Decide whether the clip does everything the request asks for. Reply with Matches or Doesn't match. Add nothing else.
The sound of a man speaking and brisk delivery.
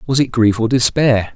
Matches